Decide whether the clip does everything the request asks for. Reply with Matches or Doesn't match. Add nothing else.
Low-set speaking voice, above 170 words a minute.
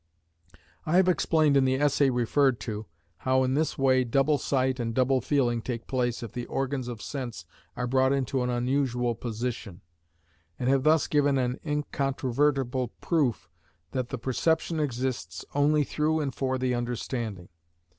Doesn't match